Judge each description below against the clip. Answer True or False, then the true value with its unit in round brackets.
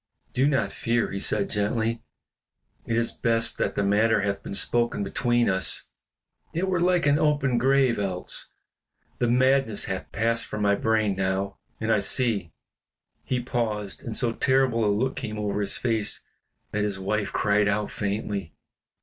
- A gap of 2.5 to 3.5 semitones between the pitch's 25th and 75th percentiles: True (3.2 semitones)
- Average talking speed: True (165 wpm)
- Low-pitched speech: True (110 Hz)